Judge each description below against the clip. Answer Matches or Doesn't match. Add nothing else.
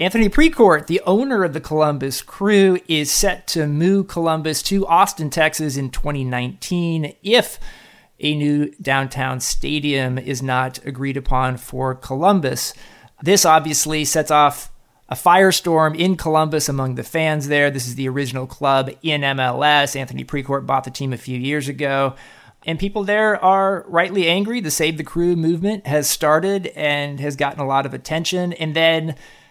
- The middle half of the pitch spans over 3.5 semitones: Matches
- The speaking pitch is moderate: Matches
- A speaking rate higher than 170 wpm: Doesn't match